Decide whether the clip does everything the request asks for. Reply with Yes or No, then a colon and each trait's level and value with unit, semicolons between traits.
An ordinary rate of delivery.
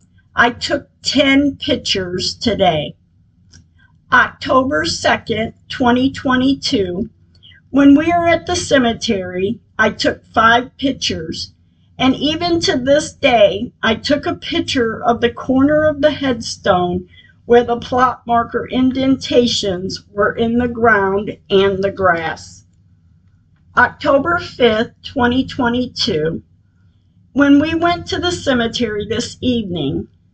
No: slow, 110 wpm